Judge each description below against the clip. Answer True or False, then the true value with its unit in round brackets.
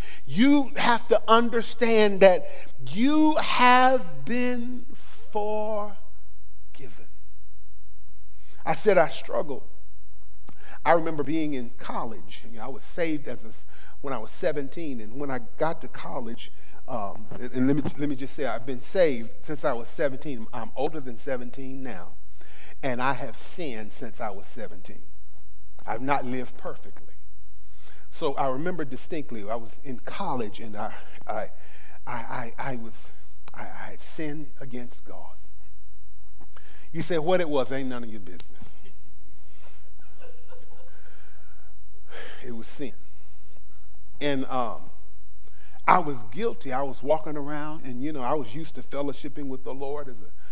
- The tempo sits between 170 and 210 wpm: False (145 wpm)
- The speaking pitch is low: True (120 Hz)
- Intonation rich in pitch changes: True (7.6 semitones)